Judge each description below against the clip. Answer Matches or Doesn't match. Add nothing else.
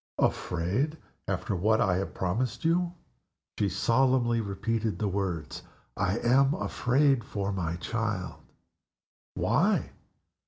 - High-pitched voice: Doesn't match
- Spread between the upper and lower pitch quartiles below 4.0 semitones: Doesn't match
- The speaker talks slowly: Matches